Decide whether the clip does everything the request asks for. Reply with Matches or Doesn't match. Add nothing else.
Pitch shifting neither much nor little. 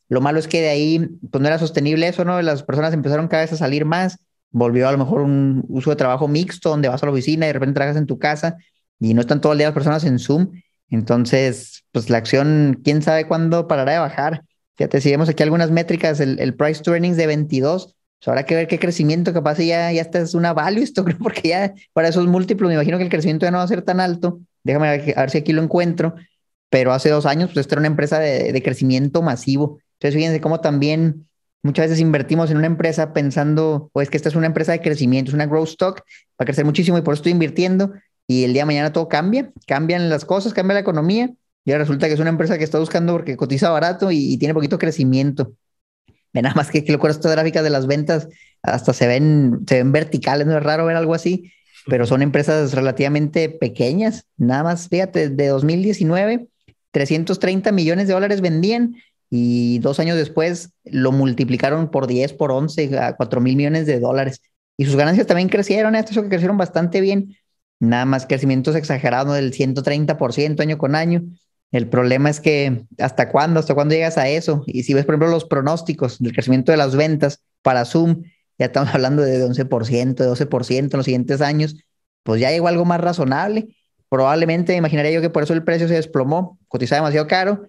Matches